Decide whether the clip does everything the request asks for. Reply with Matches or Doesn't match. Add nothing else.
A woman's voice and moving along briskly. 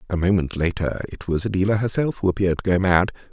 Doesn't match